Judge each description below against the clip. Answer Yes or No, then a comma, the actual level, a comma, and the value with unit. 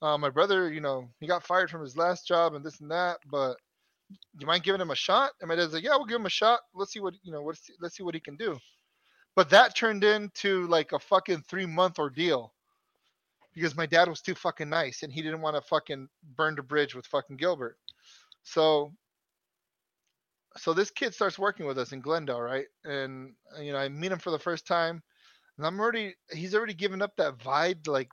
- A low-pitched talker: No, medium, 170 Hz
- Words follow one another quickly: Yes, fast, 225 wpm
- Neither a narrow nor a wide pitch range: Yes, average, 4.2 semitones